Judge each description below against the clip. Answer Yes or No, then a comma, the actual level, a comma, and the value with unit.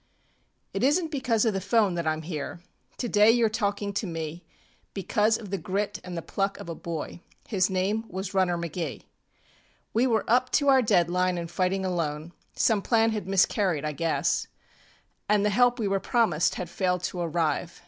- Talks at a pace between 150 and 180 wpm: No, average, 190 wpm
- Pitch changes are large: No, average, 4.2 semitones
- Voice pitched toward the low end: No, high, 190 Hz